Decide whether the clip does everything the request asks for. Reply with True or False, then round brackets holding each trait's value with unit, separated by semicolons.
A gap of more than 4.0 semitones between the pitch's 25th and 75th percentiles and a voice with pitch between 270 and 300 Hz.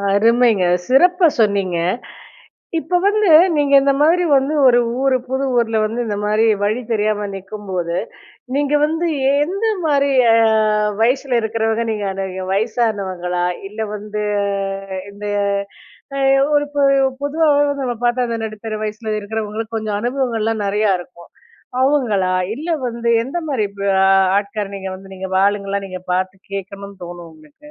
False (4.7 semitones; 220 Hz)